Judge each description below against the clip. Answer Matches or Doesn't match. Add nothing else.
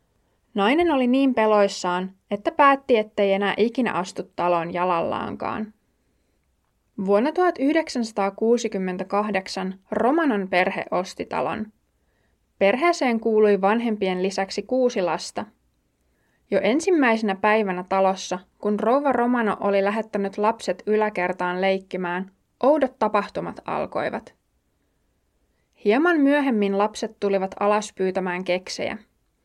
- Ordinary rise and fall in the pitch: Matches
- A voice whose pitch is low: Doesn't match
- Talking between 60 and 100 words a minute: Matches